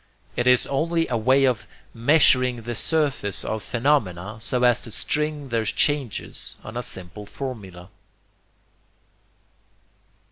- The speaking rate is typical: No, slow, 120 wpm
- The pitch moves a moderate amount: Yes, average, 4.1 semitones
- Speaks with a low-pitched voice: Yes, low, 125 Hz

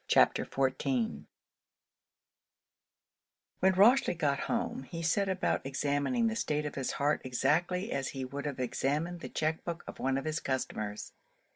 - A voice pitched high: No, medium, 150 Hz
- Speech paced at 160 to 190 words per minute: No, average, 150 wpm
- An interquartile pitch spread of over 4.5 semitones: Yes, average, 5.1 semitones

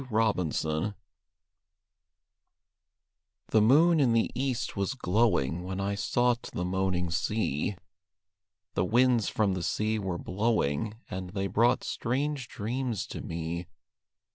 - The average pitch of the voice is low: Yes, low, 105 Hz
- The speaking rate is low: Yes, slow, 120 wpm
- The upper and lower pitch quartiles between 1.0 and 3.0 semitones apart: No, average, 4.7 semitones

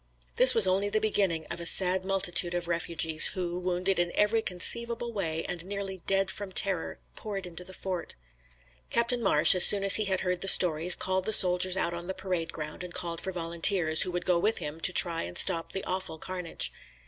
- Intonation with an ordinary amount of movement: No, narrow, 2.3 semitones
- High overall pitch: No, medium, 180 Hz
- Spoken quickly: Yes, fast, 210 wpm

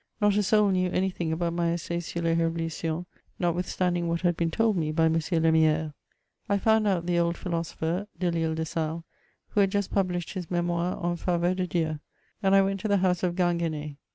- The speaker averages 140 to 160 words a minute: No, fast, 205 wpm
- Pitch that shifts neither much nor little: No, narrow, 2.1 semitones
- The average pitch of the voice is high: No, medium, 175 Hz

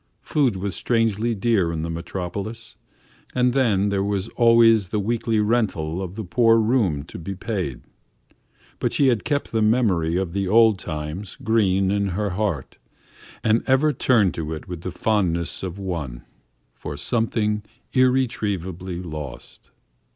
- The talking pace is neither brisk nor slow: Yes, average, 150 wpm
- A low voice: Yes, low, 100 Hz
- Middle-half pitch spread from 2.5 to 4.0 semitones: No, average, 4.4 semitones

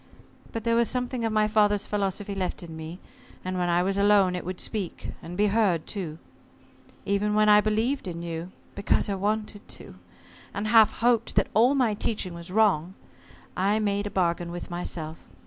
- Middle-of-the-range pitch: No, high, 200 Hz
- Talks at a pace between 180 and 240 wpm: Yes, average, 185 wpm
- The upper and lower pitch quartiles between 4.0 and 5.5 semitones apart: No, average, 3.3 semitones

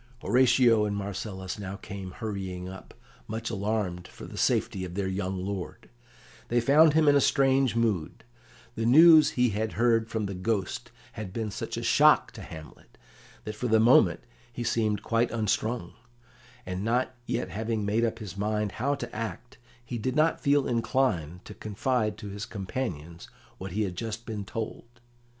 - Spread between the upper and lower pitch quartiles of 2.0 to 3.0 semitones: No, average, 3.6 semitones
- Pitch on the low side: Yes, low, 110 Hz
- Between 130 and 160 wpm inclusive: No, average, 170 wpm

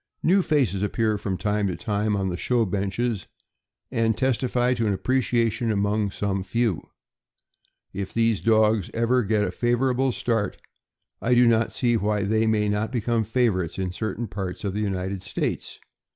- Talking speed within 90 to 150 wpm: No, average, 165 wpm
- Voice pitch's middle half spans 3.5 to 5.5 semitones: No, average, 3.0 semitones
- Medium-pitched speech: No, low, 110 Hz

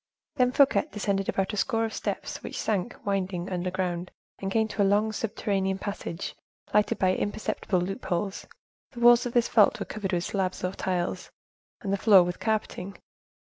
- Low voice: No, high, 195 Hz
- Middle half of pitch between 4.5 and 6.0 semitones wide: No, average, 2.8 semitones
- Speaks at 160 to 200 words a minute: Yes, average, 175 wpm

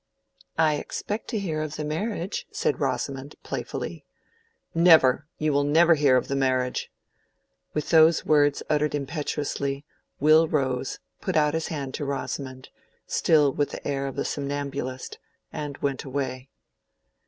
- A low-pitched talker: No, medium, 145 Hz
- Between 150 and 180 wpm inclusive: No, average, 140 wpm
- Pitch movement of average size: No, narrow, 2.1 semitones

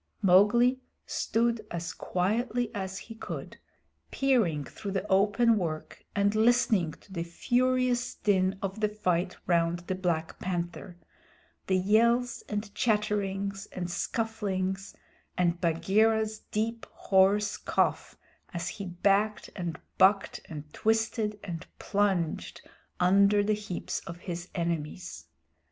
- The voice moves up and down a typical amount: Yes, average, 3.5 semitones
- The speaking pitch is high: Yes, high, 195 Hz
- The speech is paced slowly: Yes, slow, 120 wpm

